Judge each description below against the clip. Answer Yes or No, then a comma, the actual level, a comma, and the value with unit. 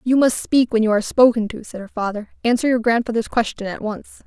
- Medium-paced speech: No, fast, 240 wpm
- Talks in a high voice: Yes, high, 230 Hz